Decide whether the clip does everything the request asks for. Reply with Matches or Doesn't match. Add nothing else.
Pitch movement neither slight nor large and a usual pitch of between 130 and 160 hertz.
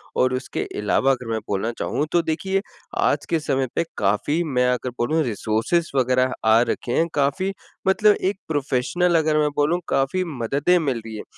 Matches